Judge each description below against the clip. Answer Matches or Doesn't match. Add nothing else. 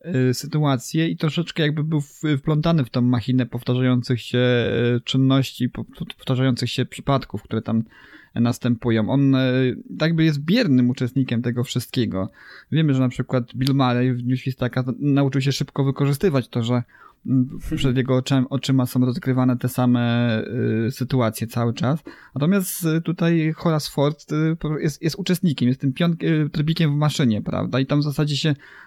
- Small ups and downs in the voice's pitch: Doesn't match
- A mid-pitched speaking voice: Doesn't match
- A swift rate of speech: Doesn't match